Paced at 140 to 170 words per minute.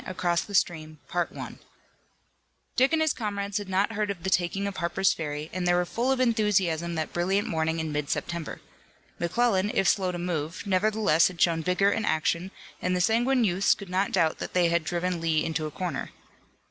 No: average, 195 wpm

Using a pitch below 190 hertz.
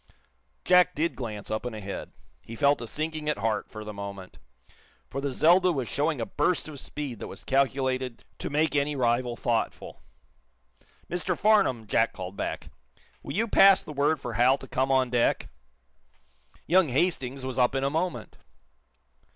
Yes: low, 135 Hz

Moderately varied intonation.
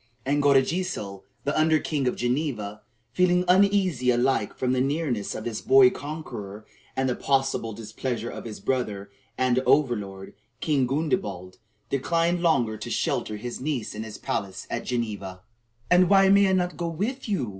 No: wide, 6.5 semitones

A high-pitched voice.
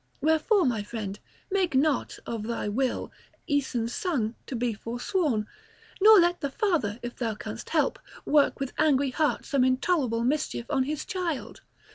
Yes: very high, 265 Hz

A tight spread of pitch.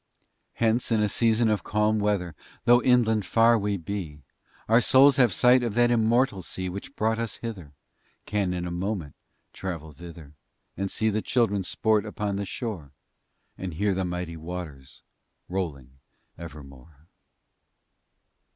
No: average, 4.6 semitones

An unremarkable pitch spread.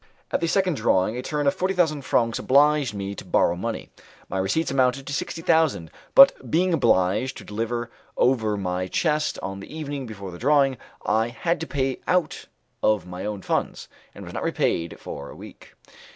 No: wide, 7.2 semitones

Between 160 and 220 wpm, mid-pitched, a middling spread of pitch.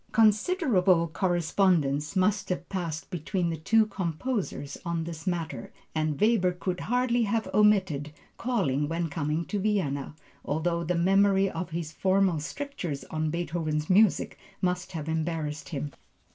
No: slow, 135 wpm; medium, 175 Hz; average, 4.0 semitones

